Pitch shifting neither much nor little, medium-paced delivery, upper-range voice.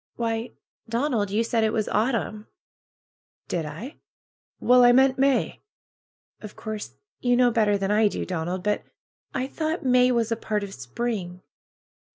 Yes: average, 3.4 semitones; average, 155 wpm; high, 225 Hz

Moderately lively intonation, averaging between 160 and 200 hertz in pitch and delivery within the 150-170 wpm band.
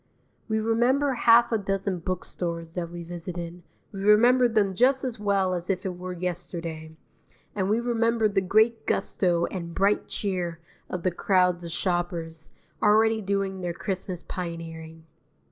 Yes: average, 3.9 semitones; medium, 185 Hz; average, 155 wpm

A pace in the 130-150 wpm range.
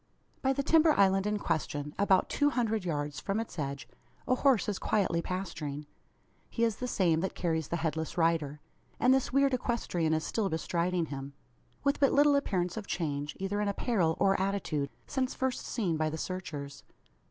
No: average, 180 wpm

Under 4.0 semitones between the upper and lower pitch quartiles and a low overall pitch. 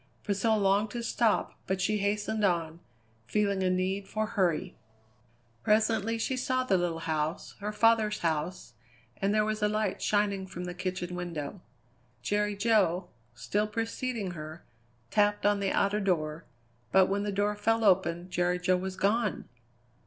No: average, 2.9 semitones; high, 200 Hz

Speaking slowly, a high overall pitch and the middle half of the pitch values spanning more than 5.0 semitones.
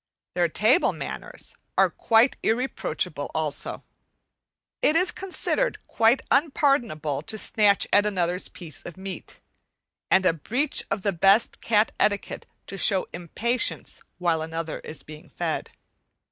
Yes: slow, 130 wpm; high, 200 Hz; wide, 5.6 semitones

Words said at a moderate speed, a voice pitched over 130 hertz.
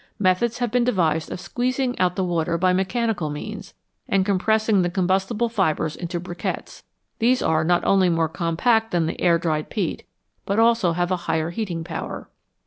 Yes: average, 175 wpm; medium, 185 Hz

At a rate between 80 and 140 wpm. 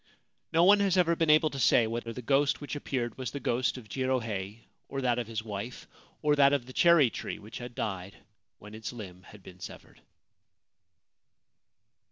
No: average, 190 wpm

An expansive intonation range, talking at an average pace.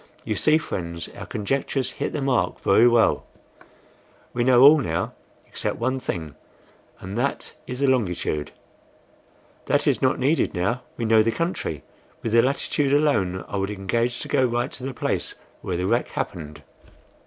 Yes: wide, 5.8 semitones; average, 165 wpm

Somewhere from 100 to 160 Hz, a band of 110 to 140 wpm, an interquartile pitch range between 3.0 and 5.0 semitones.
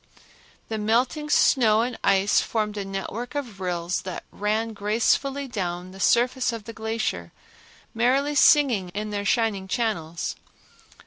No: high, 220 Hz; slow, 135 wpm; average, 3.9 semitones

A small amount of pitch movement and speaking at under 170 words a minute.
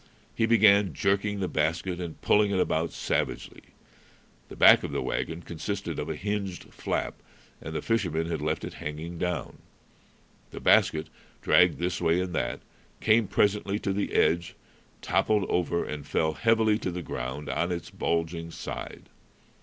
No: average, 3.9 semitones; average, 160 wpm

